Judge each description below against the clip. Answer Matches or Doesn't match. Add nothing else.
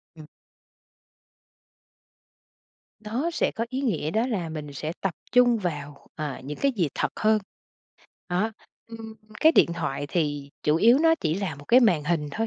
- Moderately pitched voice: Matches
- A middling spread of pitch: Doesn't match